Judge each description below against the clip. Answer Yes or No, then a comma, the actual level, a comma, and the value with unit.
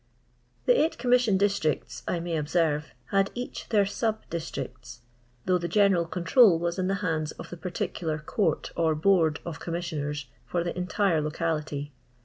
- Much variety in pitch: No, average, 4.1 semitones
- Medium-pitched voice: Yes, medium, 170 Hz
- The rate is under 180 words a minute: Yes, average, 155 wpm